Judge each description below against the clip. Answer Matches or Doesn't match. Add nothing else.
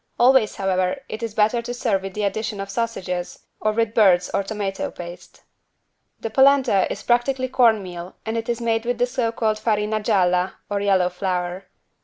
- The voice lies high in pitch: Matches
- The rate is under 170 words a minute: Doesn't match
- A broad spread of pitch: Doesn't match